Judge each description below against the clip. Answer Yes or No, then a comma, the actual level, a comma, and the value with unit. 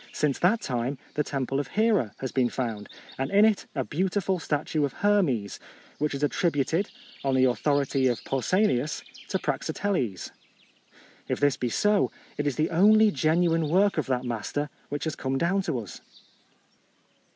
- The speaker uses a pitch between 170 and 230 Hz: No, medium, 145 Hz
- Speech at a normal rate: Yes, average, 160 wpm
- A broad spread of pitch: Yes, wide, 5.7 semitones